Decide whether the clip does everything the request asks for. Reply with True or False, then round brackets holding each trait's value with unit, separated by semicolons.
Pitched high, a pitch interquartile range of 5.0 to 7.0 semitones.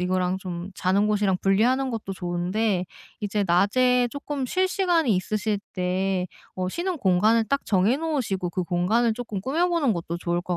True (205 Hz; 5.5 semitones)